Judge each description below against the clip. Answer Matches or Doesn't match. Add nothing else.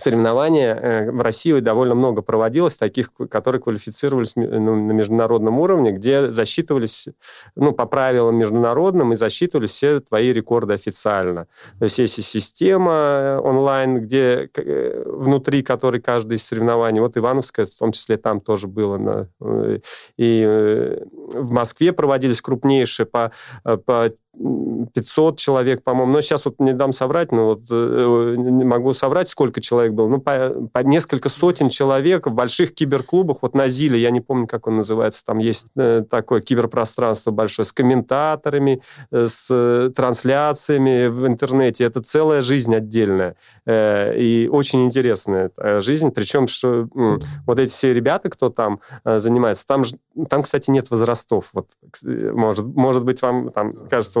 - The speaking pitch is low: Matches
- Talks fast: Doesn't match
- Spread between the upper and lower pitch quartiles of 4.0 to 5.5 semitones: Doesn't match